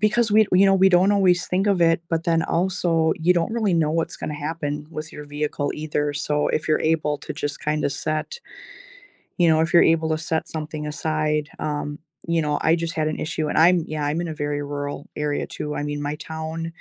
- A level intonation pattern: Yes, narrow, 2.1 semitones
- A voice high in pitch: No, medium, 160 Hz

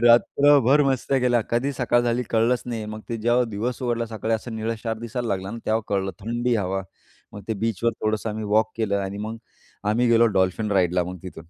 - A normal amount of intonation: No, narrow, 2.3 semitones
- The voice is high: No, low, 115 Hz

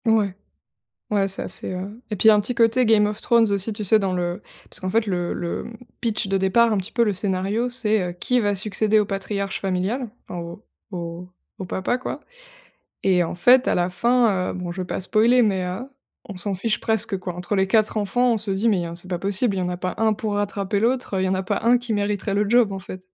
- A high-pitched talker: Yes, high, 200 Hz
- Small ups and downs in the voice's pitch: No, average, 3.2 semitones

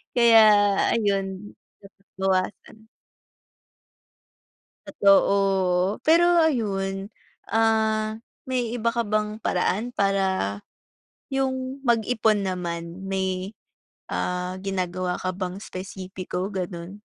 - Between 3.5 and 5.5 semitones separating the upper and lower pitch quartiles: No, average, 3.1 semitones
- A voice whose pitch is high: Yes, high, 195 Hz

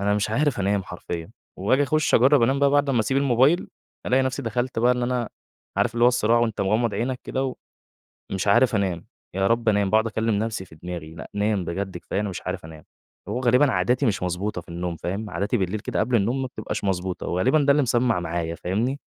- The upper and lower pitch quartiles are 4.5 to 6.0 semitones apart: Yes, average, 4.8 semitones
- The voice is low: Yes, low, 110 Hz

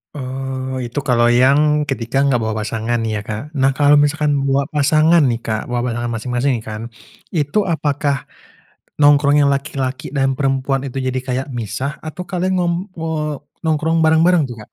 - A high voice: No, low, 135 Hz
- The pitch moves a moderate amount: Yes, average, 3.4 semitones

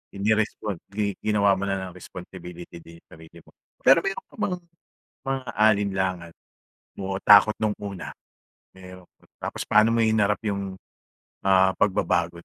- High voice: No, low, 100 Hz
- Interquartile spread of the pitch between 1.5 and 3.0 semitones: Yes, narrow, 2.6 semitones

